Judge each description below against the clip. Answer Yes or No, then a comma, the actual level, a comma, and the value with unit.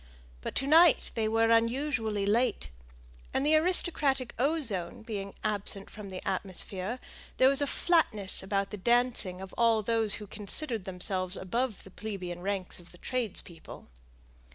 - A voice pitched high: Yes, high, 215 Hz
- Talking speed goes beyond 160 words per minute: No, average, 150 wpm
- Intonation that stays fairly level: No, average, 4.8 semitones